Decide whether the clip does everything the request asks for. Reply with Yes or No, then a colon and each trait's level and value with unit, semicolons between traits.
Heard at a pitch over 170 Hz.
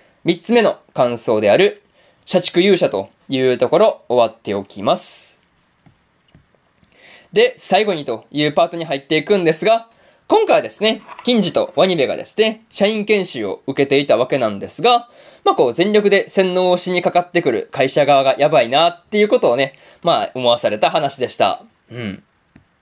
Yes: high, 190 Hz